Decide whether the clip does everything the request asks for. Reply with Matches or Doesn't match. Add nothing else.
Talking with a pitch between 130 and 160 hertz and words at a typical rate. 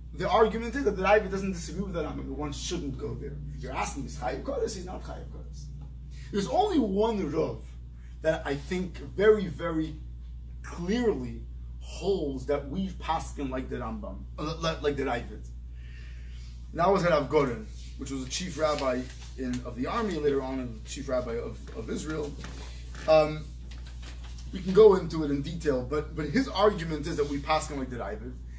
Matches